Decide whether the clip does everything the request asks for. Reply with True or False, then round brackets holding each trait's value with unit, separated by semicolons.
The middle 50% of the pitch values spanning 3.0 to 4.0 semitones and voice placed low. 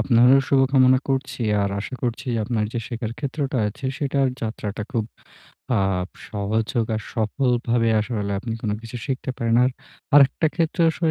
True (3.3 semitones; 120 Hz)